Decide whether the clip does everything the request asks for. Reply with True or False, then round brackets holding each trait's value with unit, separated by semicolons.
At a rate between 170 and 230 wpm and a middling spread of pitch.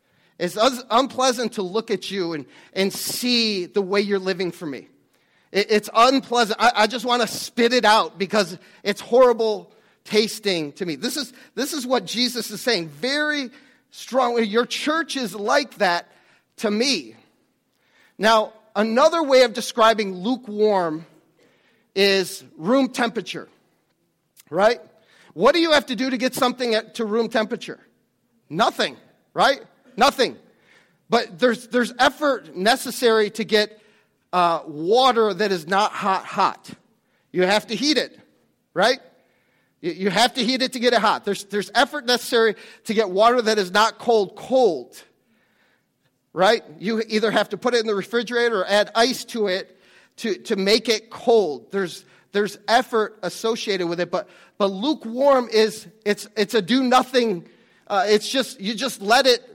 False (160 wpm; 3.4 semitones)